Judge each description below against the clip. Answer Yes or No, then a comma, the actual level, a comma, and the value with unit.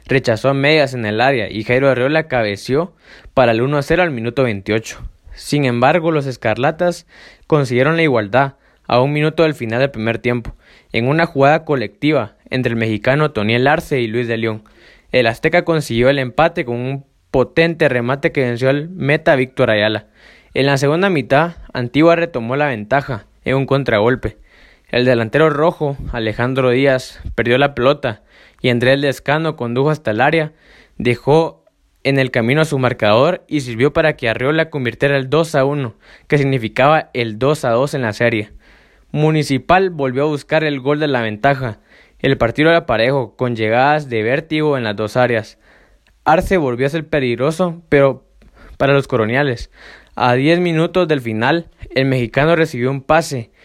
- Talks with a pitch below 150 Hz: Yes, low, 135 Hz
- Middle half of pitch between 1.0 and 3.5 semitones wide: No, average, 3.9 semitones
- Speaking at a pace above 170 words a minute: No, average, 165 wpm